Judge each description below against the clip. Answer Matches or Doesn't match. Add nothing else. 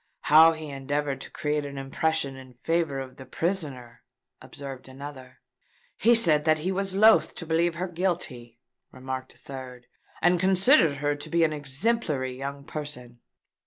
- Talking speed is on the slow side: Doesn't match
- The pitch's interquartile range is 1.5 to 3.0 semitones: Doesn't match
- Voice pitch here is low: Doesn't match